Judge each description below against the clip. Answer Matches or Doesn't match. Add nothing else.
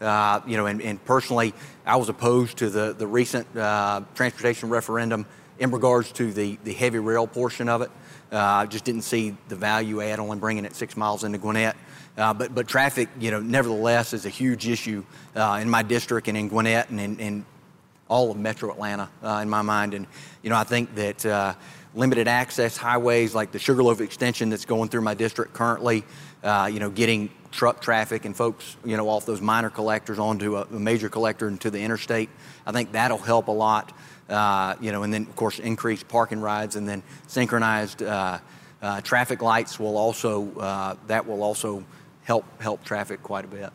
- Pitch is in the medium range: Doesn't match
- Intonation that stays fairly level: Matches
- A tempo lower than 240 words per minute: Matches